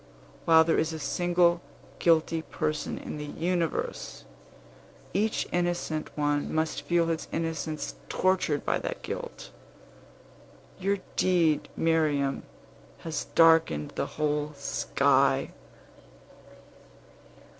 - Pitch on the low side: No, medium, 160 Hz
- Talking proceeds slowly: Yes, slow, 100 wpm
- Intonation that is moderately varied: No, narrow, 2.2 semitones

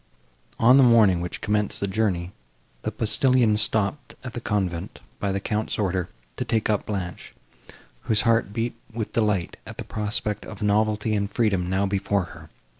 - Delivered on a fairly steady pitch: Yes, narrow, 2.3 semitones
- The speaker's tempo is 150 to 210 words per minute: Yes, average, 170 wpm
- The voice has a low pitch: Yes, low, 105 Hz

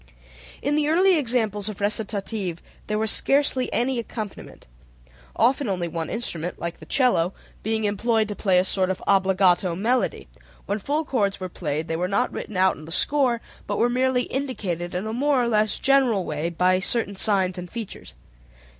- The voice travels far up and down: No, average, 5.0 semitones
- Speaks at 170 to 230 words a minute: Yes, average, 180 wpm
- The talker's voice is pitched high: Yes, high, 210 Hz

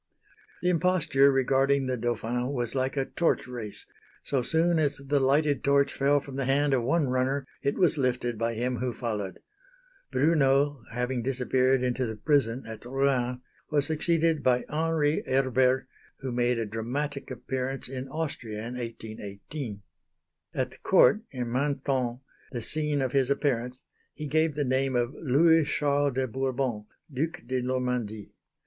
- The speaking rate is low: No, average, 155 wpm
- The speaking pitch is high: No, low, 130 Hz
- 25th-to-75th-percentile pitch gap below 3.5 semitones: Yes, narrow, 2.6 semitones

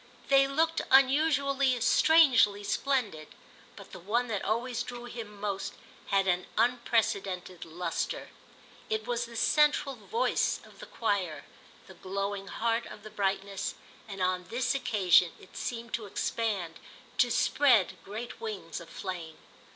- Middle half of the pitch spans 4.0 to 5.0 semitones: Yes, average, 4.4 semitones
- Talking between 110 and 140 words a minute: Yes, slow, 135 wpm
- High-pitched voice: Yes, high, 220 Hz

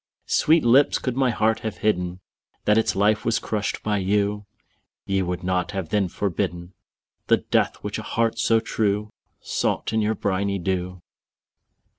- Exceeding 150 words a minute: Yes, average, 170 wpm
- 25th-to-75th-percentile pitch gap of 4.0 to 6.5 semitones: No, average, 3.0 semitones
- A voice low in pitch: Yes, low, 105 Hz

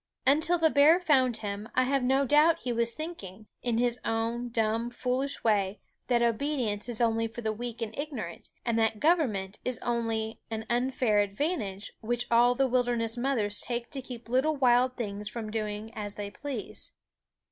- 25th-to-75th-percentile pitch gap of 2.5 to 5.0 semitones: Yes, average, 2.9 semitones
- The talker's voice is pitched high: Yes, high, 235 Hz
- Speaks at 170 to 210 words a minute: Yes, average, 175 wpm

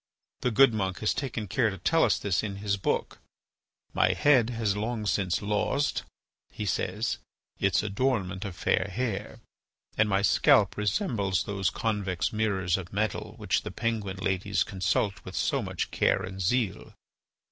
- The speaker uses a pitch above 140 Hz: No, low, 100 Hz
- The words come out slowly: No, average, 160 wpm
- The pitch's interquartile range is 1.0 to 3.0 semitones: Yes, narrow, 2.6 semitones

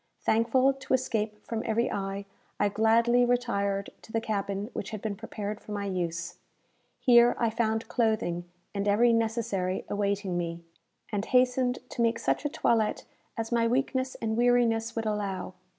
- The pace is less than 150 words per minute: No, average, 160 wpm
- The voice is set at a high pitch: Yes, high, 220 Hz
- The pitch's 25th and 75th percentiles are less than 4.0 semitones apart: Yes, average, 2.9 semitones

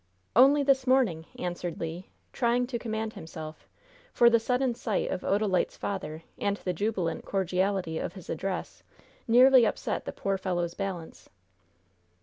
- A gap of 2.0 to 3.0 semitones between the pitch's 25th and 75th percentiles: No, average, 5.3 semitones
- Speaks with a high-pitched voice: Yes, high, 195 Hz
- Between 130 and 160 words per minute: Yes, average, 140 wpm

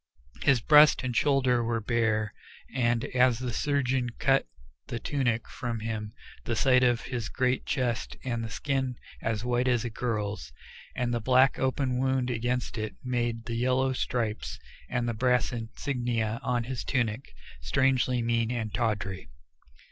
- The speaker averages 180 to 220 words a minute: No, average, 155 wpm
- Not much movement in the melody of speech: Yes, narrow, 2.1 semitones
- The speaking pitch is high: No, low, 120 Hz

